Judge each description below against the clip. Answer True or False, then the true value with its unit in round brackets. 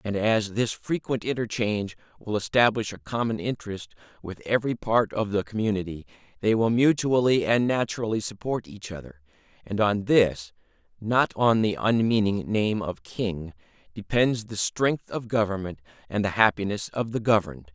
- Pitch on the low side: True (105 Hz)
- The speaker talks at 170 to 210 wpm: False (150 wpm)